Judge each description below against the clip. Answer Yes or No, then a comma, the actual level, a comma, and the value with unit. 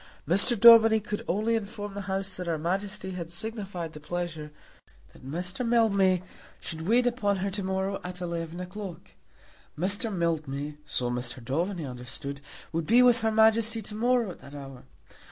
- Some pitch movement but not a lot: Yes, average, 4.8 semitones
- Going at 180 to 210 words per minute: No, average, 165 wpm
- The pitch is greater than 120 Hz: Yes, high, 190 Hz